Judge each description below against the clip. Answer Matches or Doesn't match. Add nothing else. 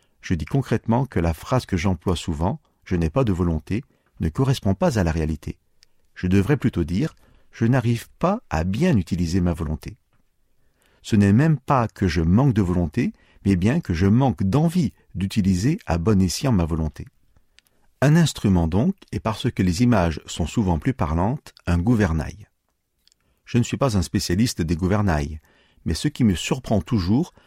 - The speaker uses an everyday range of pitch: Doesn't match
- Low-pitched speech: Matches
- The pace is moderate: Matches